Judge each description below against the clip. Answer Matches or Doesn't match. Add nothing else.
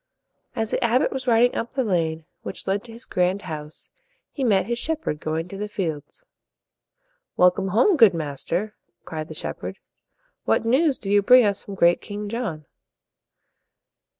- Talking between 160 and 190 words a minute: Matches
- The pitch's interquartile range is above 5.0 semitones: Matches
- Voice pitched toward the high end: Matches